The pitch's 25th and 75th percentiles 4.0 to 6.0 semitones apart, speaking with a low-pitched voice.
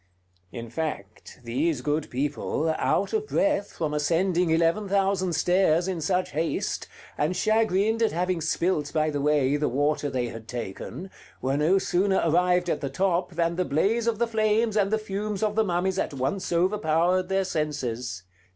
No: average, 4.7 semitones; medium, 170 Hz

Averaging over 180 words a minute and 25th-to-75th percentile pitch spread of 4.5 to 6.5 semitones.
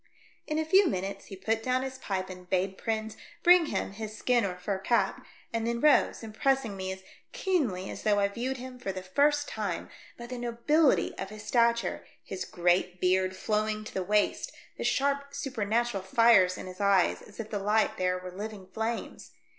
Yes: average, 195 wpm; average, 4.8 semitones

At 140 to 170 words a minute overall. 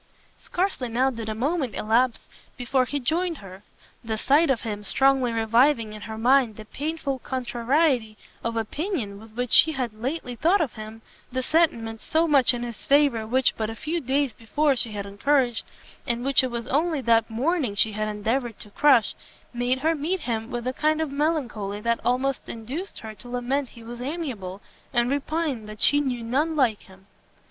No: average, 190 wpm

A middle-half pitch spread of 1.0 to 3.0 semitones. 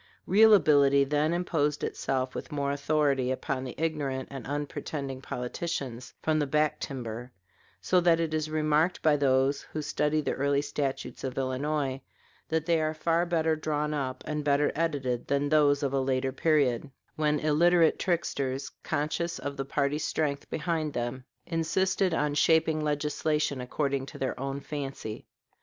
Yes: narrow, 2.4 semitones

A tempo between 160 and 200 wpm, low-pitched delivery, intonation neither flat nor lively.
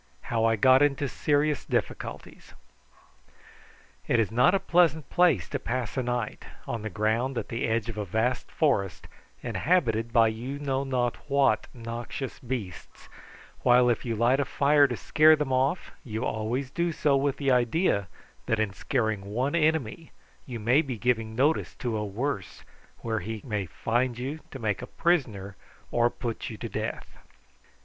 Yes: average, 170 wpm; low, 125 Hz; average, 4.0 semitones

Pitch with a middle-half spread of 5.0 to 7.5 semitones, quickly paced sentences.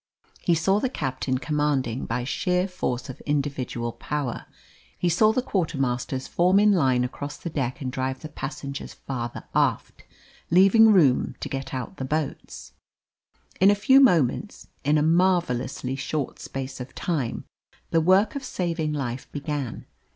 No: wide, 5.5 semitones; average, 150 wpm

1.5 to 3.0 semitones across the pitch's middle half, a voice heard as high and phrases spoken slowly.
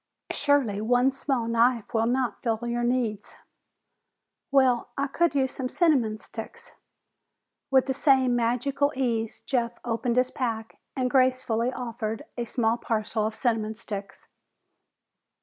Yes: average, 2.7 semitones; high, 245 Hz; slow, 130 wpm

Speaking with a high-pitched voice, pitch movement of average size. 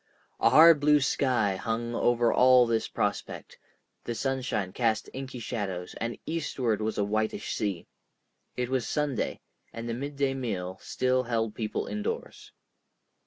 No: low, 120 Hz; average, 3.3 semitones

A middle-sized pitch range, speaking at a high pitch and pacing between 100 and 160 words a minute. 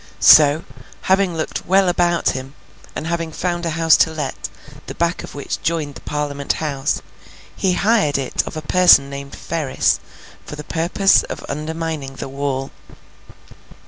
No: average, 3.3 semitones; medium, 160 Hz; average, 155 wpm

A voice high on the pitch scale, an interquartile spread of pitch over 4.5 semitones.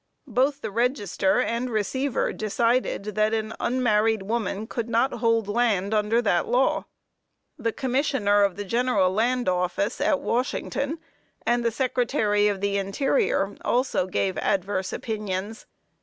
No: high, 220 Hz; average, 3.5 semitones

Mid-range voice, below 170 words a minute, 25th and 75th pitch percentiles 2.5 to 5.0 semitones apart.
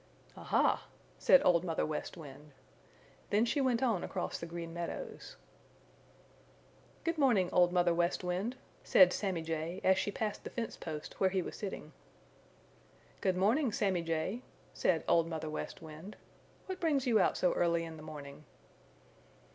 Yes: medium, 180 Hz; average, 155 wpm; average, 4.6 semitones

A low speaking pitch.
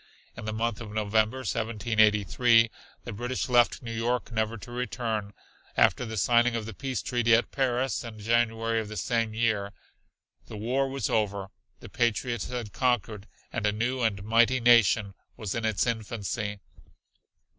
Yes: low, 115 Hz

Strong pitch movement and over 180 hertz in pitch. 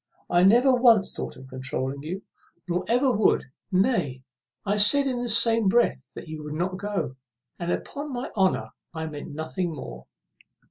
Yes: wide, 7.3 semitones; high, 190 Hz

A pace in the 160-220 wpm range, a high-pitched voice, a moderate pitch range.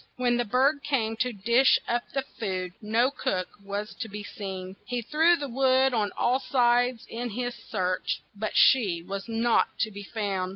Yes: average, 180 wpm; high, 230 Hz; average, 3.8 semitones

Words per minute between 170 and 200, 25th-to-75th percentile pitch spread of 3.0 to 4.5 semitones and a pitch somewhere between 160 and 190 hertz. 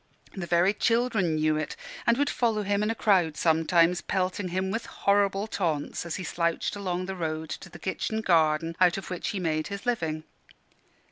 Yes: average, 190 wpm; average, 3.7 semitones; medium, 185 Hz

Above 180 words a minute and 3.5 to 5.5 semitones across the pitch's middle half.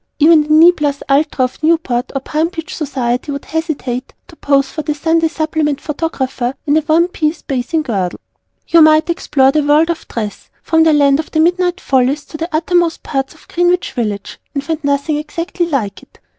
No: average, 195 wpm; average, 2.9 semitones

